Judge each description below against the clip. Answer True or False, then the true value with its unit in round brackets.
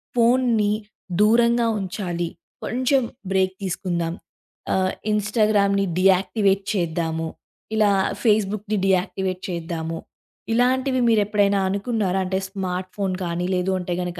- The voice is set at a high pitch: True (195 Hz)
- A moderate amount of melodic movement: True (3.0 semitones)